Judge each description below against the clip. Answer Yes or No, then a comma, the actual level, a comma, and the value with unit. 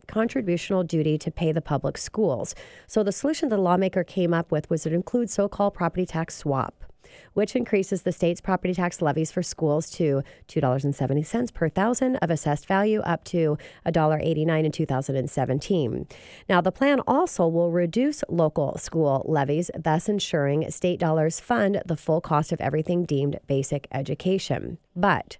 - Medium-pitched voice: Yes, medium, 170 Hz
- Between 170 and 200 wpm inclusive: No, average, 160 wpm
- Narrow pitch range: No, average, 3.8 semitones